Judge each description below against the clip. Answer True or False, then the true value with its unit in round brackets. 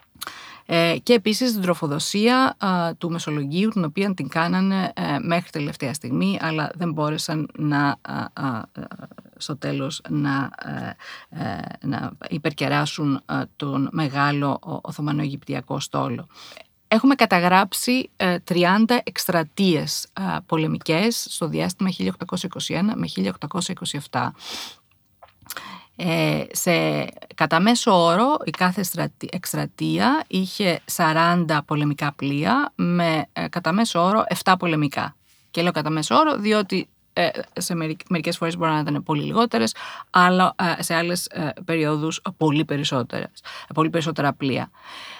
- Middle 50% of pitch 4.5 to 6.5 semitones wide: False (4.0 semitones)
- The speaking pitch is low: False (165 Hz)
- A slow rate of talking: True (110 wpm)